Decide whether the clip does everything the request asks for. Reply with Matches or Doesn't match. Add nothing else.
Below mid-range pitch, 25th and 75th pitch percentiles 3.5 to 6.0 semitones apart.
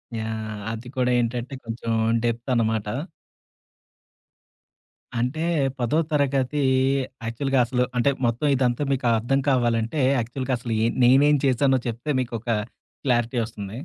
Doesn't match